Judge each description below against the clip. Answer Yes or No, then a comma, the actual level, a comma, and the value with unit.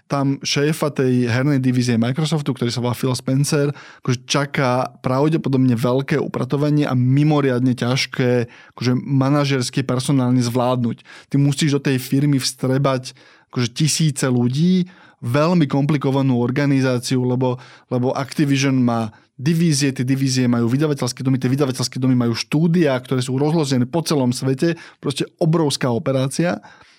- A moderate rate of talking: Yes, average, 130 wpm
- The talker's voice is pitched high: No, low, 135 Hz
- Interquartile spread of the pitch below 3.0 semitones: Yes, narrow, 2.5 semitones